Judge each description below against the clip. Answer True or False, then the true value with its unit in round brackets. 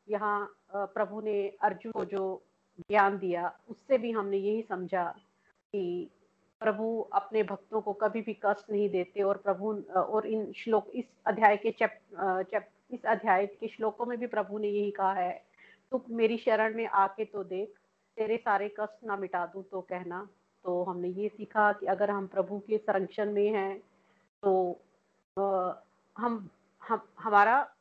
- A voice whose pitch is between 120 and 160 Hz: False (205 Hz)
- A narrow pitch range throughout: True (1.9 semitones)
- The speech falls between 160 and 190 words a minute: True (165 wpm)